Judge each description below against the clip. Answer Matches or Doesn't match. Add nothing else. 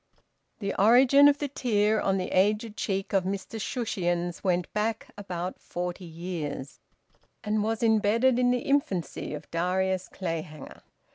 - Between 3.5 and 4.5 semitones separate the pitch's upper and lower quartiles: Matches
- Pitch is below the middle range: Doesn't match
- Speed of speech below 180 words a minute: Matches